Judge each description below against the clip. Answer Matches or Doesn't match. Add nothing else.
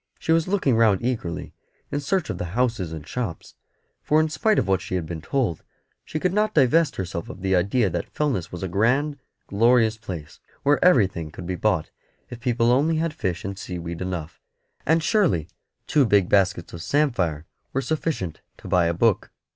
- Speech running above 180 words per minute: Matches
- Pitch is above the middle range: Doesn't match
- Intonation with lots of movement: Matches